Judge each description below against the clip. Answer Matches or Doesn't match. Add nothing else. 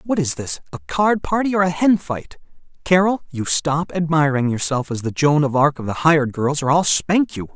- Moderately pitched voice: Matches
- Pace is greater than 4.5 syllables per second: Matches